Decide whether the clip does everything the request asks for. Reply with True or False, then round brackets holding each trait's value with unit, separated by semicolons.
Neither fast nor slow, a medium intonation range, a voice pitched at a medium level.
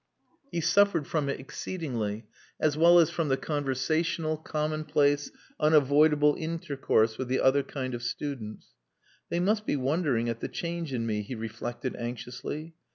True (150 wpm; 4.1 semitones; 145 Hz)